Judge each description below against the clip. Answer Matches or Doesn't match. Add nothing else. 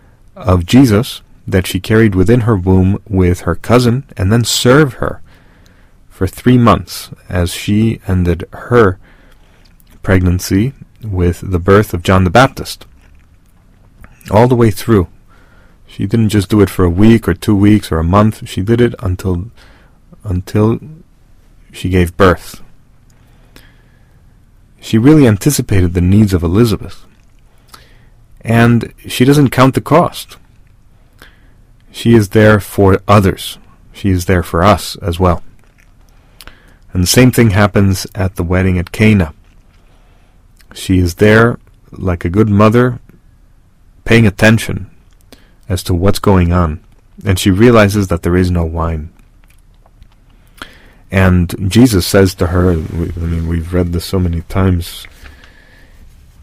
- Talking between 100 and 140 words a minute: Matches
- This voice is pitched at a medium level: Doesn't match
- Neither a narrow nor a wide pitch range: Matches